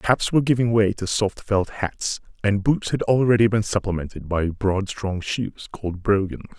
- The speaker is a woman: No, male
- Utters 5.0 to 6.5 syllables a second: No, 4.6 syllables/s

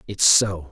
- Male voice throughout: Yes, male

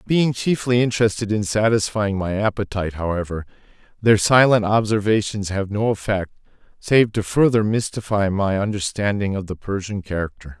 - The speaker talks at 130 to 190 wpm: Yes, slow, 135 wpm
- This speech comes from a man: Yes, male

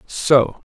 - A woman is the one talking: No, male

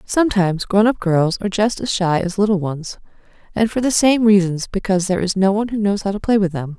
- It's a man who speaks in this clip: No, female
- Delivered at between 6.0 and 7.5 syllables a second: Yes, 6.2 syllables/s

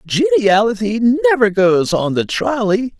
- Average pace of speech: No, slow, 120 wpm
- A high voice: Yes, high, 220 Hz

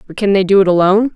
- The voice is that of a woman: Yes, female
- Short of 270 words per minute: No, fast, 310 wpm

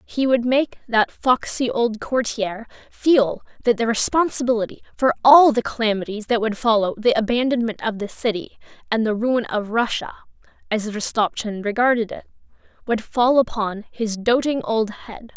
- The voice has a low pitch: No, high, 230 Hz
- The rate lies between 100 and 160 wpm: Yes, average, 150 wpm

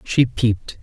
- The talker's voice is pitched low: Yes, low, 120 Hz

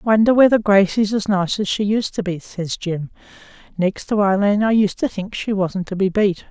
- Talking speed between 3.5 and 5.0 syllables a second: Yes, 4.9 syllables/s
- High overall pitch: Yes, high, 200 Hz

